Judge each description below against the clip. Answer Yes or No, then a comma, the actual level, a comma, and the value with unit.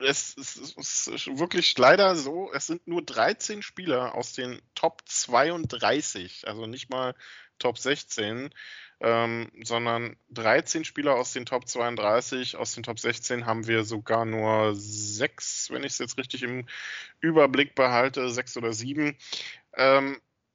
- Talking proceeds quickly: No, average, 145 wpm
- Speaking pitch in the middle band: No, low, 125 Hz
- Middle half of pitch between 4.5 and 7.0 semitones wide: No, average, 3.0 semitones